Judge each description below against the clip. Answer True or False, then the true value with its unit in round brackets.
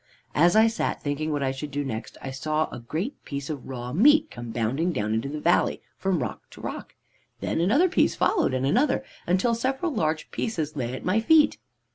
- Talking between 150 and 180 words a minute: False (205 wpm)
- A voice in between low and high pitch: True (155 Hz)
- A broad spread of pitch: True (8.8 semitones)